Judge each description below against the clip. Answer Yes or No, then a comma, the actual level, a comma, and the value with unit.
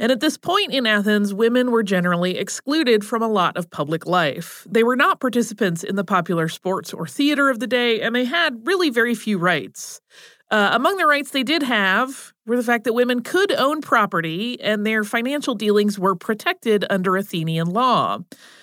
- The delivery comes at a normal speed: Yes, average, 195 wpm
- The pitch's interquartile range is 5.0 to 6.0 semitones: Yes, average, 5.3 semitones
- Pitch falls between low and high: No, high, 230 Hz